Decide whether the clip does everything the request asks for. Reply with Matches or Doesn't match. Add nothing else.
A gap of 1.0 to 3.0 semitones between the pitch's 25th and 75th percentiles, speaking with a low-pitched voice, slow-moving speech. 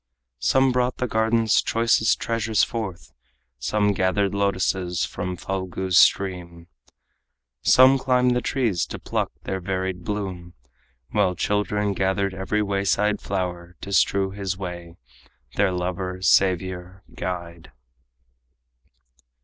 Matches